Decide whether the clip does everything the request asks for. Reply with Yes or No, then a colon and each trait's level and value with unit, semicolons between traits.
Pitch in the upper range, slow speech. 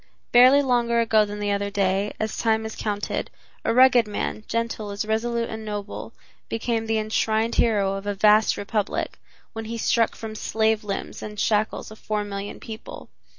No: high, 220 Hz; average, 175 wpm